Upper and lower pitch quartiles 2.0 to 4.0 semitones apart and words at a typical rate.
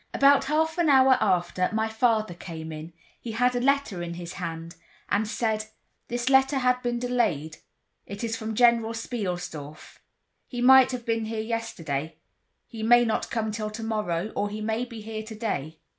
No: average, 5.0 semitones; average, 165 wpm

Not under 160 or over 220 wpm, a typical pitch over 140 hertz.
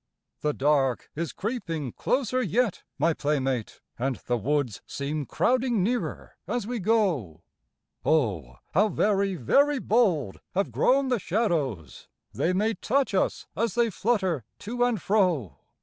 No: slow, 135 wpm; medium, 185 Hz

